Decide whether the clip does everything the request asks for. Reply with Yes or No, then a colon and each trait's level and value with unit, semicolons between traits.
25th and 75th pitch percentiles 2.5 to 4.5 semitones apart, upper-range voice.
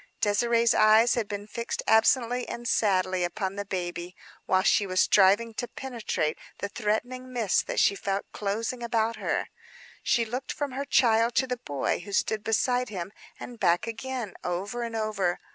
Yes: average, 3.4 semitones; high, 220 Hz